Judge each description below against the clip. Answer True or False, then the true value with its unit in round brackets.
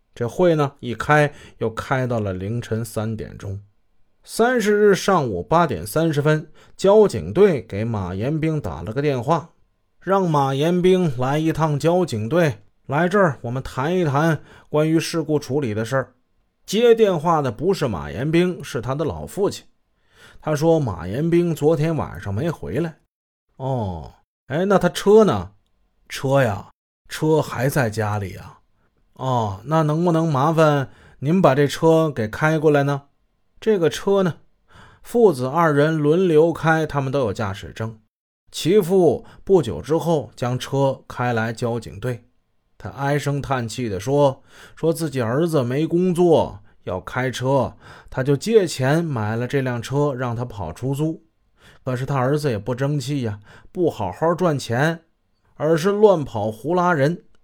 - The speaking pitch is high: False (140 Hz)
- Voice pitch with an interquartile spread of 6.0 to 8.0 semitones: True (6.3 semitones)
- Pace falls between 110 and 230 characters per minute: True (215 characters per minute)